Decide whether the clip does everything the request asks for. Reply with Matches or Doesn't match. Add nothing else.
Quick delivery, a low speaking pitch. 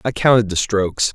Matches